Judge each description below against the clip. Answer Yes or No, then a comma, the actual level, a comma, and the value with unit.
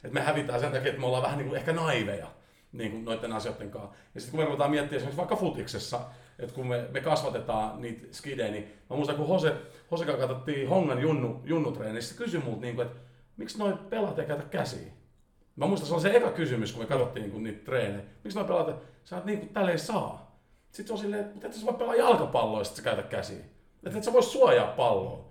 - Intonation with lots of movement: Yes, wide, 6.8 semitones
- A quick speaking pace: Yes, fast, 235 wpm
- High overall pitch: No, medium, 140 Hz